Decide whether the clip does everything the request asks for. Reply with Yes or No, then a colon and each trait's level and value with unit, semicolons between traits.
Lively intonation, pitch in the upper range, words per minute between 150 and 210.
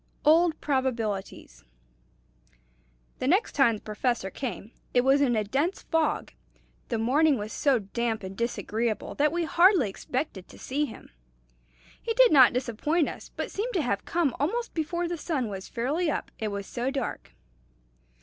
Yes: wide, 6.2 semitones; very high, 265 Hz; average, 160 wpm